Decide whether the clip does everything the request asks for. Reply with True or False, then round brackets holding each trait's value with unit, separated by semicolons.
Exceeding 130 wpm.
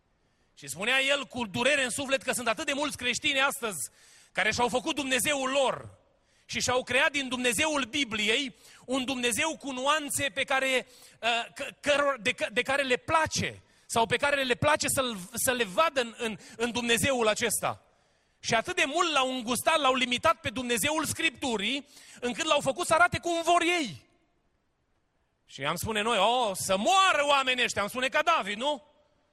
True (165 wpm)